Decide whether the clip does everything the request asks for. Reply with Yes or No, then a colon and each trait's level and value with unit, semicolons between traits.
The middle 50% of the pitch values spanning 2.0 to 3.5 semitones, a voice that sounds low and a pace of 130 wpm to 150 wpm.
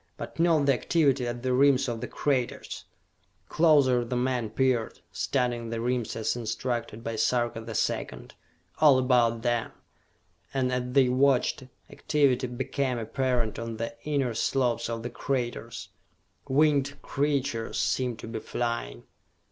Yes: narrow, 2.5 semitones; low, 125 Hz; average, 140 wpm